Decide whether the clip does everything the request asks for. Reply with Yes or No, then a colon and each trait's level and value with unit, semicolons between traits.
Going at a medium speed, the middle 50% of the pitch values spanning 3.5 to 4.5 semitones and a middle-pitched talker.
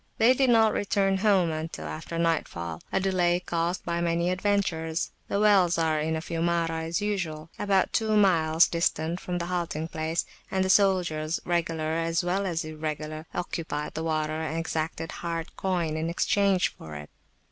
No: average, 170 wpm; average, 2.7 semitones; medium, 170 Hz